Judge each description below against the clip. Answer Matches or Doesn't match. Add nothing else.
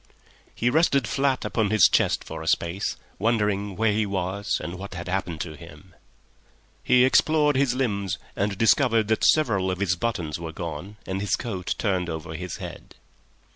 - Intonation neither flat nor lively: Matches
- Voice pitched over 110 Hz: Doesn't match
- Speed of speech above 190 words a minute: Doesn't match